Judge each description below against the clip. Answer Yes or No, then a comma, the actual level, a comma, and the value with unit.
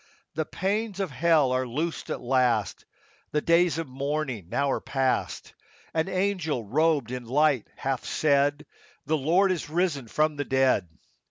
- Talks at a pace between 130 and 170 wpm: Yes, average, 165 wpm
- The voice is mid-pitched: Yes, medium, 145 Hz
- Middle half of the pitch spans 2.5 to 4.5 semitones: Yes, average, 4.1 semitones